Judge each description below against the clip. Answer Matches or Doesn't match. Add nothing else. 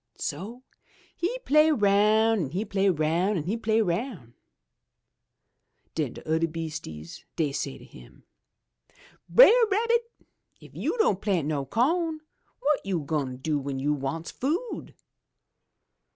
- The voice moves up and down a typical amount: Doesn't match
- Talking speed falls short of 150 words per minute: Matches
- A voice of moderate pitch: Doesn't match